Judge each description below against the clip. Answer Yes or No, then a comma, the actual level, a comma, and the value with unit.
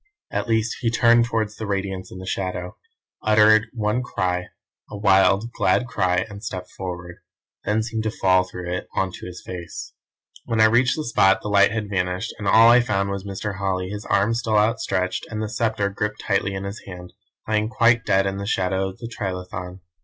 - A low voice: Yes, low, 100 Hz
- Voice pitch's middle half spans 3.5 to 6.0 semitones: No, average, 2.9 semitones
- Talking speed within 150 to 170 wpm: No, average, 200 wpm